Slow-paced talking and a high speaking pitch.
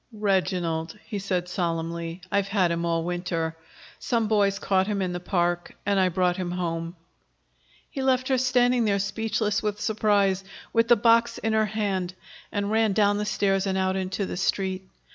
No: average, 180 wpm; high, 195 Hz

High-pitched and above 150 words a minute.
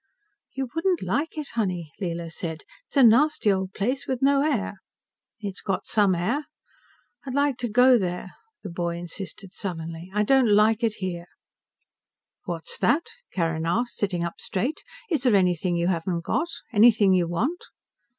Yes: high, 200 Hz; average, 160 wpm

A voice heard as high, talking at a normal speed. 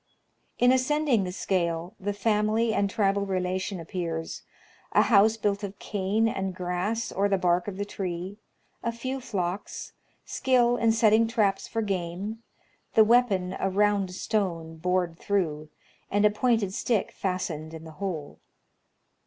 Yes: high, 200 Hz; average, 150 wpm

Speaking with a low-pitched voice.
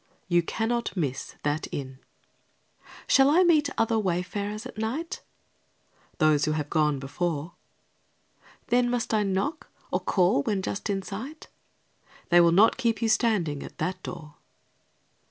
No: high, 195 Hz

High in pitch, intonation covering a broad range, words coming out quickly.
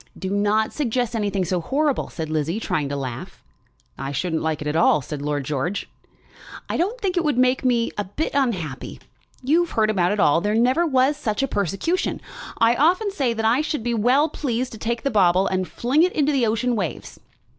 Yes: high, 225 Hz; wide, 7.2 semitones; fast, 210 wpm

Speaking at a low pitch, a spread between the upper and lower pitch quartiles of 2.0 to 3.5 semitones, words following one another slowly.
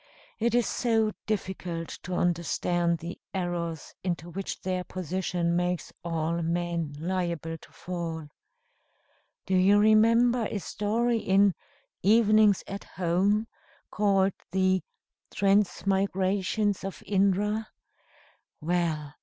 No: medium, 185 Hz; average, 3.1 semitones; slow, 105 wpm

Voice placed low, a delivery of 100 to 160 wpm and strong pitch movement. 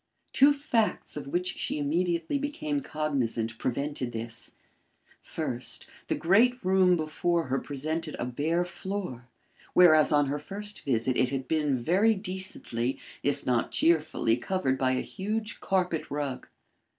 No: medium, 155 Hz; average, 140 wpm; wide, 6.2 semitones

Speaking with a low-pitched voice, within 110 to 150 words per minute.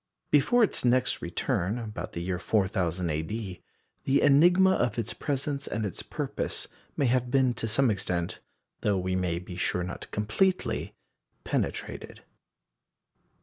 Yes: low, 110 Hz; average, 140 wpm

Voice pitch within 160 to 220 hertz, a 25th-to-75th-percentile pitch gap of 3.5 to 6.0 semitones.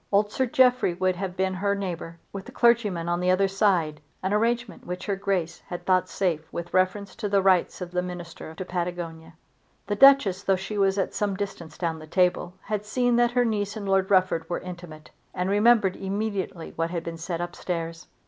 No: medium, 185 Hz; average, 2.7 semitones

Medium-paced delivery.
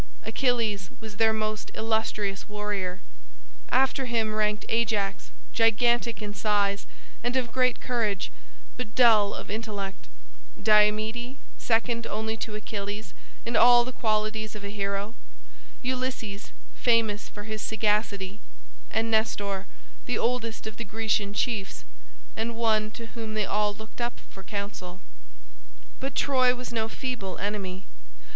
No: slow, 130 wpm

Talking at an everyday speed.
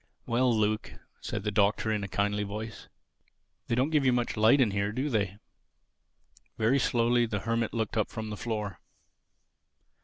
Yes: average, 165 wpm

